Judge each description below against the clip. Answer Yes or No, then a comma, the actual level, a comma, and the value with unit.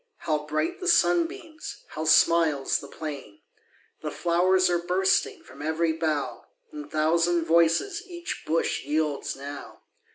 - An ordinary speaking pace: No, slow, 130 wpm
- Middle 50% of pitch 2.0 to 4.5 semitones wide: Yes, average, 3.7 semitones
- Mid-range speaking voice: Yes, medium, 165 Hz